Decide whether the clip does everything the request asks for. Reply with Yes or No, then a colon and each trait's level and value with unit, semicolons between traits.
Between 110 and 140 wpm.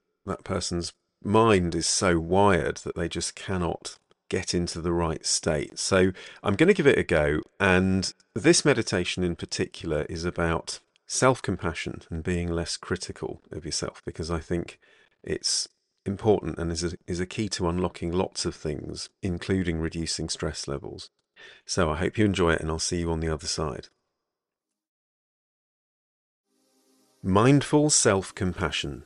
No: average, 155 wpm